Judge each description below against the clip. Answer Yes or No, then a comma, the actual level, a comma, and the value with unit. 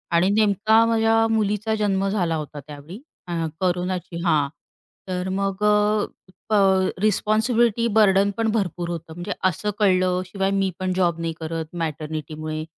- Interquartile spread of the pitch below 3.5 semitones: No, average, 3.8 semitones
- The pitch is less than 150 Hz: No, high, 190 Hz